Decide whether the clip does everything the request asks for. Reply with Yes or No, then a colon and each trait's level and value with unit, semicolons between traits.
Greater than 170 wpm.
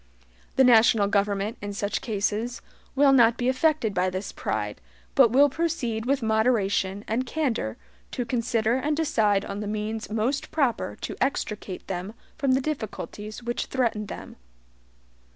No: average, 150 wpm